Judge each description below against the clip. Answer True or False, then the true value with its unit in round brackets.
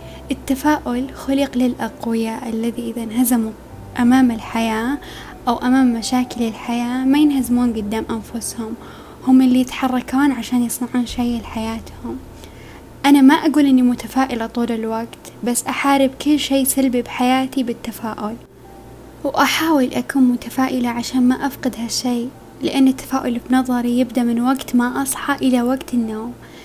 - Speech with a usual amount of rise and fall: False (2.1 semitones)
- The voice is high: True (250 Hz)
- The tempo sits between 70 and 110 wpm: False (125 wpm)